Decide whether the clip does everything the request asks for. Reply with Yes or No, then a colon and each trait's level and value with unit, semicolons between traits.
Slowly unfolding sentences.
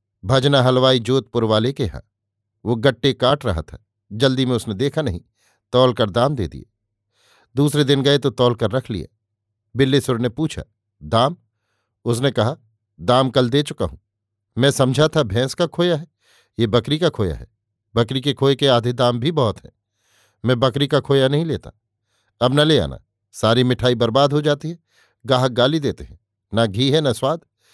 No: average, 185 wpm